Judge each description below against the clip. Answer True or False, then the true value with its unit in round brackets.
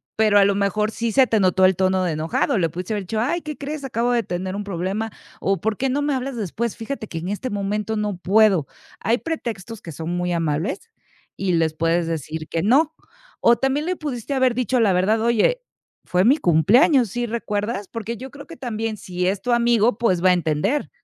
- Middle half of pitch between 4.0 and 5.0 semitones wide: True (4.7 semitones)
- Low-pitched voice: False (210 Hz)